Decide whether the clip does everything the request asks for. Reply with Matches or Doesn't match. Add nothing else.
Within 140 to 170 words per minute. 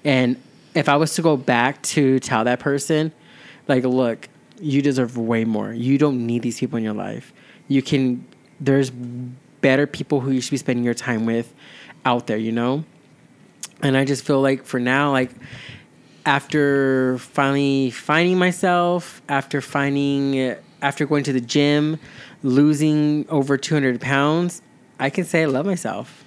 Matches